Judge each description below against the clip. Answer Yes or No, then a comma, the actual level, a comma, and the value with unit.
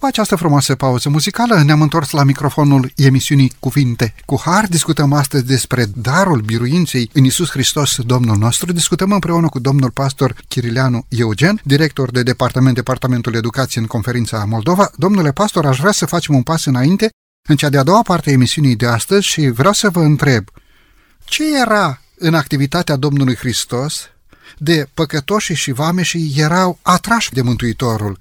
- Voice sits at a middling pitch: Yes, medium, 145 Hz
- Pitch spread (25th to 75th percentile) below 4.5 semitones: No, average, 4.9 semitones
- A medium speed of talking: Yes, average, 160 wpm